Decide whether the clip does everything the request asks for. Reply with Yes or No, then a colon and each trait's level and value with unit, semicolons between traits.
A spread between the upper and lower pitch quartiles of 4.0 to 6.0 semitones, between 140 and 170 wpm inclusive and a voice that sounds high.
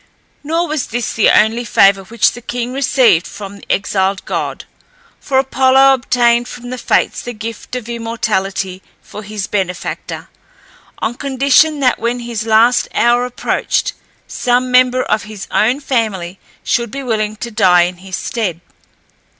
No: average, 3.4 semitones; average, 150 wpm; high, 235 Hz